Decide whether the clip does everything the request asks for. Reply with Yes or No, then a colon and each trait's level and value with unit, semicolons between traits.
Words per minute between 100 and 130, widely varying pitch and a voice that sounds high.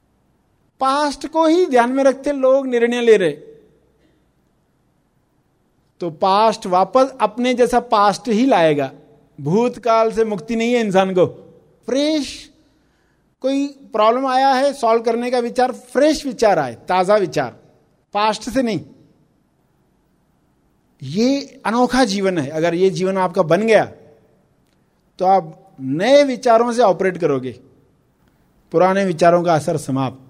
Yes: average, 125 wpm; wide, 6.8 semitones; high, 220 Hz